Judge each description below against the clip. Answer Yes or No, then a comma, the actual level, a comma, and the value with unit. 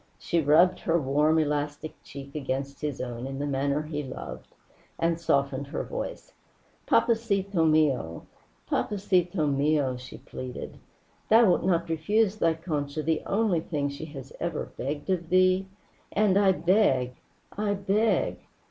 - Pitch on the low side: No, medium, 155 Hz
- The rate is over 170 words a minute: No, average, 140 wpm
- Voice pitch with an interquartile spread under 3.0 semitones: No, average, 4.8 semitones